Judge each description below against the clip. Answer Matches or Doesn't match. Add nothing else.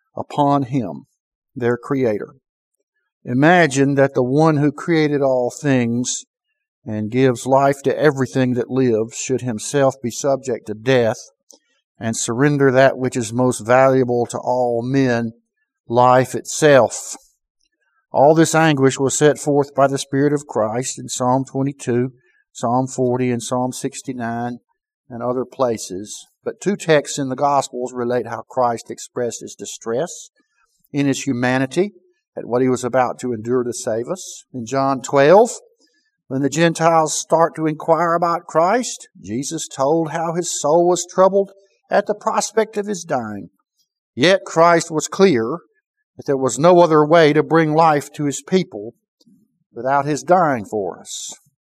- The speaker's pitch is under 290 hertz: Matches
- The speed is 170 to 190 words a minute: Doesn't match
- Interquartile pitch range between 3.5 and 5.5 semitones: Matches